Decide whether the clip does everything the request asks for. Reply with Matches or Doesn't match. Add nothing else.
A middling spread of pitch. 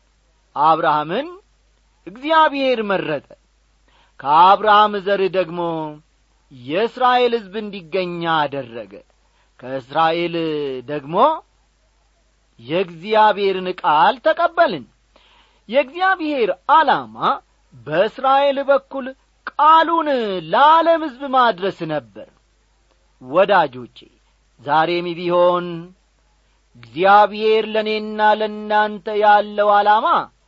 Doesn't match